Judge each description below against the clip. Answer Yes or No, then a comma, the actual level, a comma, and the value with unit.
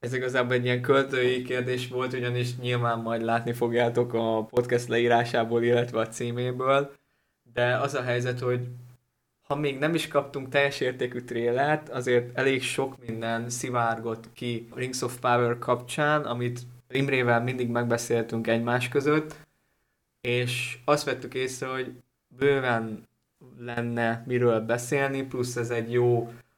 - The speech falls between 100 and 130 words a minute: No, average, 140 wpm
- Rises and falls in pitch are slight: Yes, narrow, 1.5 semitones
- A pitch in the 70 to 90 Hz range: No, low, 125 Hz